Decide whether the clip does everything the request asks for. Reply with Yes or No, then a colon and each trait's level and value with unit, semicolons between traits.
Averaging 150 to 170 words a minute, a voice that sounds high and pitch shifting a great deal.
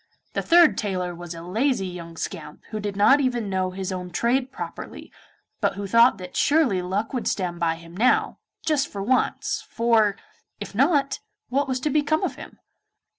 No: average, 180 wpm; high, 210 Hz; wide, 6.3 semitones